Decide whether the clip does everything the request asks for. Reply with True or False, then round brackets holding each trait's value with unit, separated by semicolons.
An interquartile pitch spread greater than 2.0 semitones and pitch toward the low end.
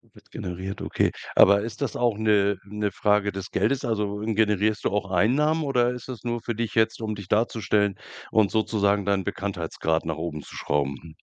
True (2.5 semitones; 105 Hz)